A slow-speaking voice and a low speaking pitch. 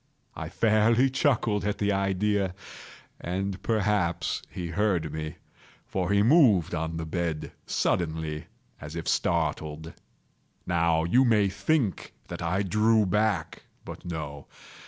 Yes: slow, 120 wpm; very low, 95 Hz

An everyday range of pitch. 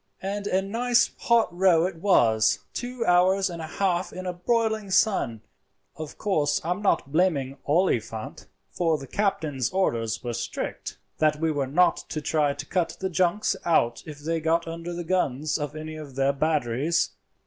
Yes: average, 4.5 semitones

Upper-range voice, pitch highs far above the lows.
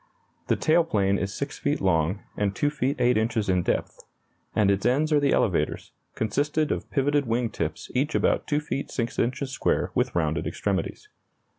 No: low, 125 Hz; wide, 6.2 semitones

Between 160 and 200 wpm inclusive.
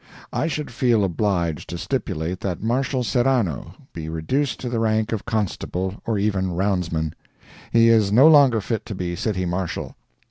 Yes: average, 165 wpm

